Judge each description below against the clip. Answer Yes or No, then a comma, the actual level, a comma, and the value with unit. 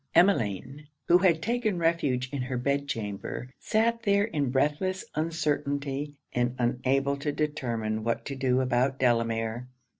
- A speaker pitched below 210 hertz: Yes, medium, 140 Hz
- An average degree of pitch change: Yes, average, 4.4 semitones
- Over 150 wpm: No, average, 140 wpm